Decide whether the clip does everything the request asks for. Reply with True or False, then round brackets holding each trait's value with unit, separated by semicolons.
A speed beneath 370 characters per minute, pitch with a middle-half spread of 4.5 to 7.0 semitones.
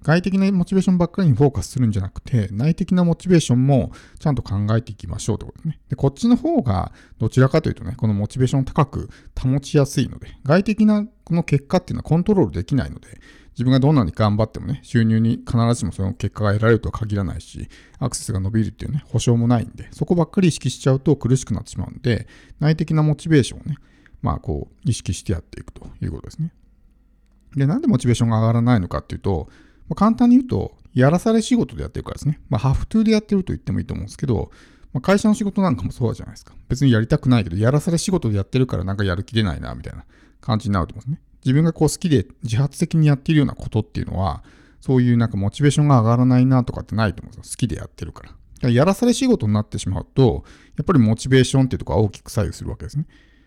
False (550 characters per minute; 6.1 semitones)